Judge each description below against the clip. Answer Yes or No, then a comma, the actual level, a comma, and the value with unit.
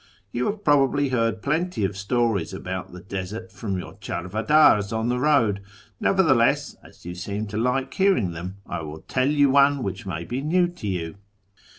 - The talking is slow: No, average, 180 wpm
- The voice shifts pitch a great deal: Yes, wide, 6.6 semitones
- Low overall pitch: Yes, low, 115 Hz